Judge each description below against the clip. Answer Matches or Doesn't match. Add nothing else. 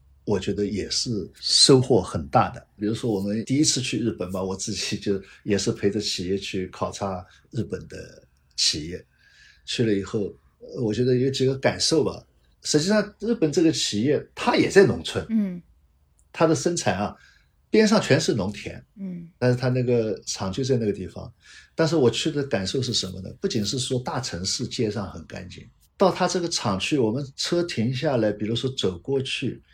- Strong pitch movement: Matches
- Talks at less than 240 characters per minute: Doesn't match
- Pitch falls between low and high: Doesn't match